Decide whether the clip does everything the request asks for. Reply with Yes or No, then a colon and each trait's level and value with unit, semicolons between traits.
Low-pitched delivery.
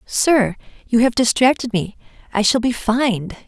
No: high, 235 Hz